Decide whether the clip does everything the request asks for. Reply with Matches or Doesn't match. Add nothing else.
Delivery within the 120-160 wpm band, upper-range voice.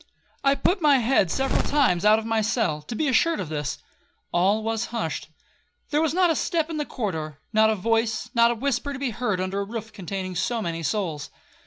Doesn't match